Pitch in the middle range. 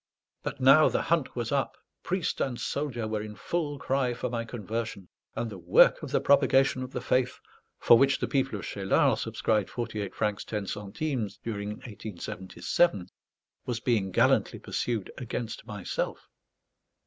No: low, 115 Hz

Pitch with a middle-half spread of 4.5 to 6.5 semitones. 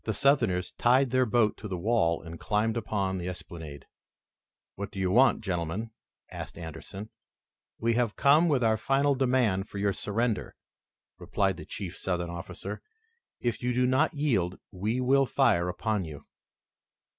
Yes: average, 5.2 semitones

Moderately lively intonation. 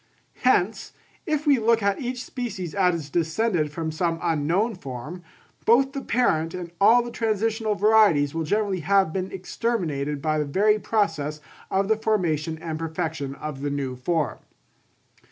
No: wide, 5.9 semitones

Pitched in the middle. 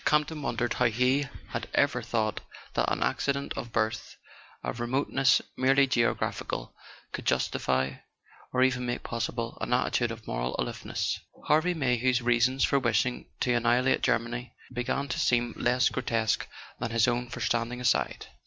No: low, 125 Hz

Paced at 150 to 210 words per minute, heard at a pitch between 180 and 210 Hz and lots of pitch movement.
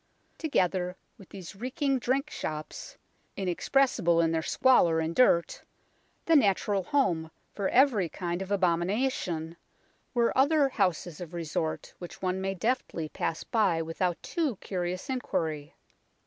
No: slow, 135 wpm; medium, 185 Hz; wide, 6.9 semitones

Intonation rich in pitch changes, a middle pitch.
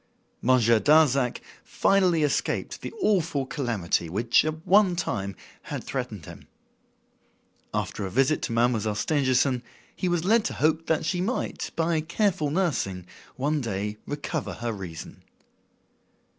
Yes: wide, 6.2 semitones; medium, 145 Hz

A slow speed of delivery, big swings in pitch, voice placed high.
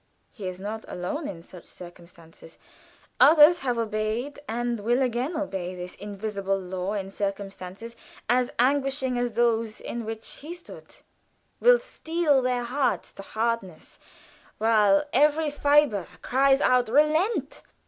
Yes: slow, 130 wpm; wide, 5.7 semitones; high, 235 Hz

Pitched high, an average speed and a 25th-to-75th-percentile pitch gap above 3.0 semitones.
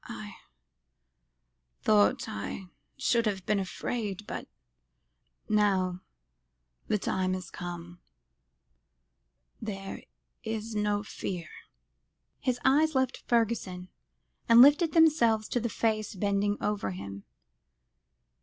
No: high, 210 Hz; slow, 100 wpm; average, 4.0 semitones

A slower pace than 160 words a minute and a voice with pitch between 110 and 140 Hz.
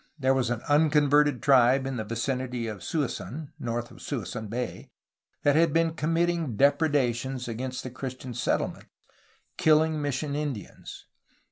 Yes: average, 140 wpm; low, 135 Hz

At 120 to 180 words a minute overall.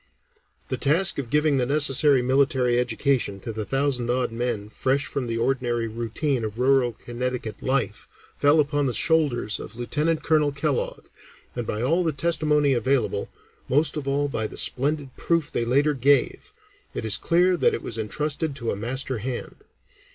Yes: average, 170 wpm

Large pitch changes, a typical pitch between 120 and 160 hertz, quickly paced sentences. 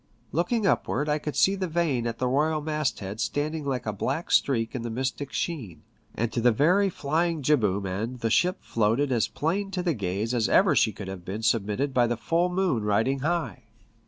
Yes: wide, 6.1 semitones; low, 135 Hz; fast, 210 wpm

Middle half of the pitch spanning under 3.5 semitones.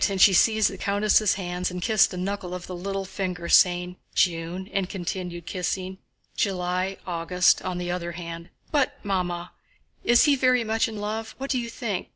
Yes: average, 2.7 semitones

